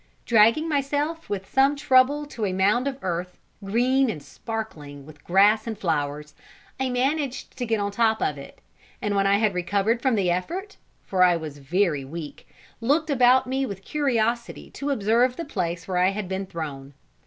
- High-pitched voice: Yes, high, 215 Hz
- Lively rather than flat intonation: Yes, wide, 6.3 semitones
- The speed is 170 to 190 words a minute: Yes, average, 180 wpm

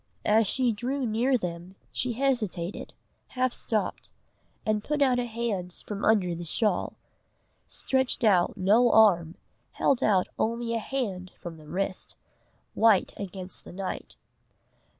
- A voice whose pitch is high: Yes, high, 215 Hz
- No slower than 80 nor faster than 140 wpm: Yes, slow, 135 wpm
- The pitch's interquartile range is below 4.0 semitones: No, average, 4.6 semitones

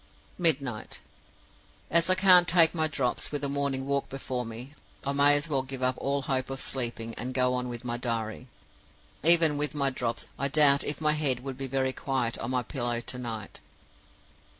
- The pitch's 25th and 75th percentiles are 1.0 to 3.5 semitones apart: Yes, narrow, 2.6 semitones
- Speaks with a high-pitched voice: No, low, 135 Hz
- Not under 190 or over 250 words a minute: Yes, average, 195 wpm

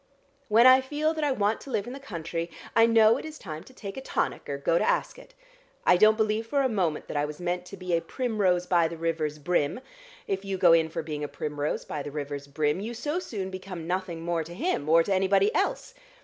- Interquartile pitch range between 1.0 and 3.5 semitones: No, wide, 5.6 semitones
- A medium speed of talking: No, fast, 245 wpm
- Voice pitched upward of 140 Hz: Yes, medium, 185 Hz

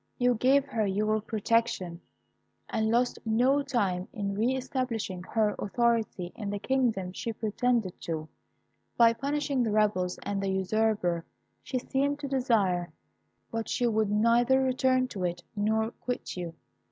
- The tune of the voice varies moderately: Yes, average, 4.0 semitones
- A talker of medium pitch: No, high, 220 Hz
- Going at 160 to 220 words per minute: No, average, 145 wpm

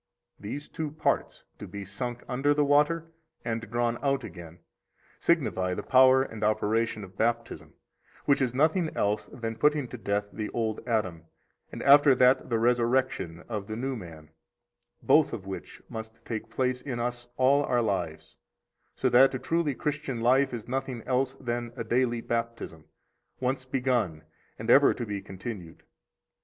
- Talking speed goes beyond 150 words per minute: Yes, average, 160 wpm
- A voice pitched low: Yes, low, 120 Hz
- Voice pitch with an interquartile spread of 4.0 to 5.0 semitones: No, average, 3.6 semitones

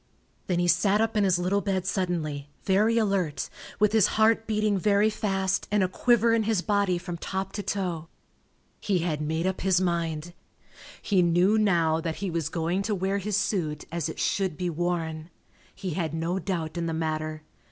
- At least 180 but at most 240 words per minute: Yes, average, 190 wpm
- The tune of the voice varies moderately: Yes, average, 3.4 semitones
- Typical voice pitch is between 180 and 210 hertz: Yes, medium, 185 Hz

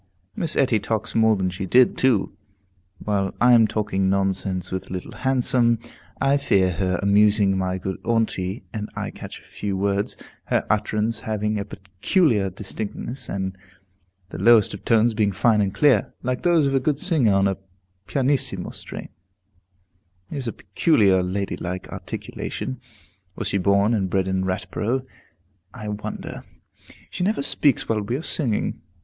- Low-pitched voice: Yes, low, 105 Hz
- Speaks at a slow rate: No, average, 155 wpm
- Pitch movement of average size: Yes, average, 4.0 semitones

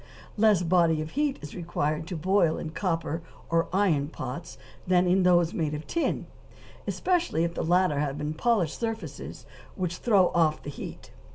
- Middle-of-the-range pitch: Yes, medium, 175 Hz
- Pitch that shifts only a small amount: No, average, 3.2 semitones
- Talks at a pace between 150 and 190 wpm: Yes, average, 165 wpm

